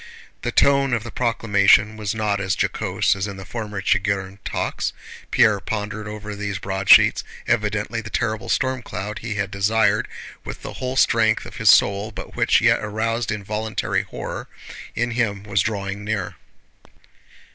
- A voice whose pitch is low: Yes, low, 105 Hz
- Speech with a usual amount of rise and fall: No, narrow, 1.9 semitones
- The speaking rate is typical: Yes, average, 155 wpm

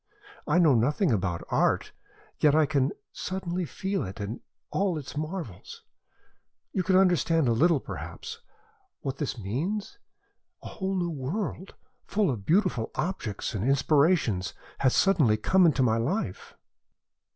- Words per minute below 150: Yes, average, 140 wpm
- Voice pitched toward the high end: No, medium, 155 Hz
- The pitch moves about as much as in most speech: No, wide, 7.7 semitones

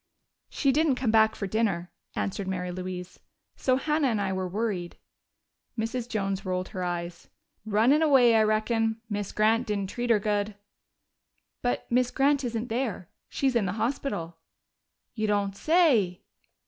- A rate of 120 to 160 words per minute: Yes, average, 150 wpm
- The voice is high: Yes, high, 215 Hz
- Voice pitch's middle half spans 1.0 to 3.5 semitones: No, average, 4.4 semitones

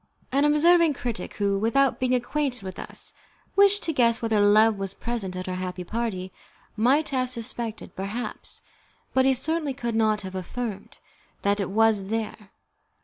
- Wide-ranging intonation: No, average, 4.5 semitones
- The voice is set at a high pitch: Yes, high, 225 Hz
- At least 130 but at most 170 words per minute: Yes, average, 160 wpm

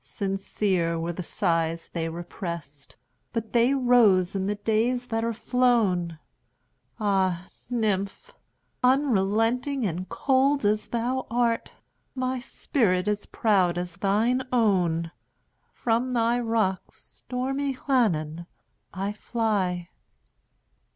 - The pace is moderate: No, slow, 95 wpm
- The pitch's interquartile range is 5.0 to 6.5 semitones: Yes, average, 5.3 semitones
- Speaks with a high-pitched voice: Yes, high, 210 Hz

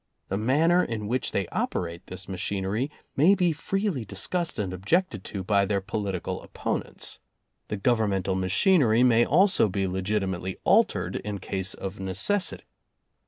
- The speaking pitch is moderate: No, low, 105 Hz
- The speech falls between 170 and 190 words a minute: No, average, 150 wpm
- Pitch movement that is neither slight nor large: No, wide, 6.0 semitones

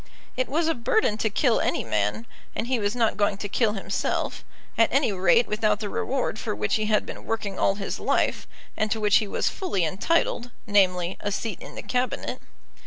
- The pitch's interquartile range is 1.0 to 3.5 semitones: Yes, average, 3.2 semitones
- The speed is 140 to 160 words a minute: No, fast, 205 wpm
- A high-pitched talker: Yes, high, 215 Hz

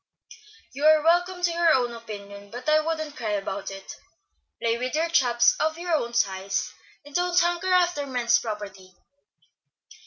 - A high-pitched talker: Yes, very high, 255 Hz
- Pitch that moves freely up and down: Yes, wide, 7.8 semitones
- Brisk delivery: No, average, 150 wpm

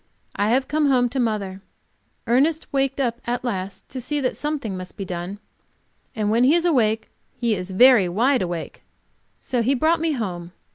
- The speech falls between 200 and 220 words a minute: No, average, 185 wpm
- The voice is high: Yes, high, 240 Hz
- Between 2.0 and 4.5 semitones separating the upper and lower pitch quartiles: No, wide, 5.6 semitones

